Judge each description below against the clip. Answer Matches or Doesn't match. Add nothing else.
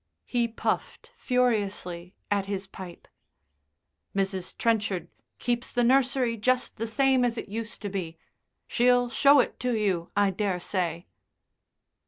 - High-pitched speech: Matches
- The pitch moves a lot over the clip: Doesn't match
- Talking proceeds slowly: Matches